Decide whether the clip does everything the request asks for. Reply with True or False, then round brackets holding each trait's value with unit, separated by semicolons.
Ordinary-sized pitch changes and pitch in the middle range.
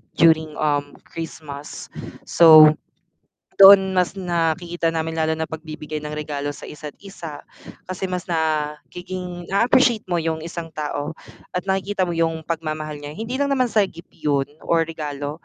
True (3.0 semitones; 160 Hz)